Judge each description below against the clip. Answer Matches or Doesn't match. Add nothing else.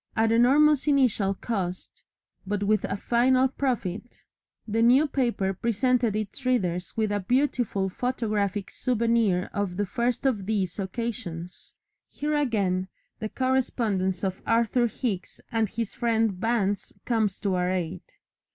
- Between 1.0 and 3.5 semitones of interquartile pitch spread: Doesn't match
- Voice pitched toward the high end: Matches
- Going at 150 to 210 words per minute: Doesn't match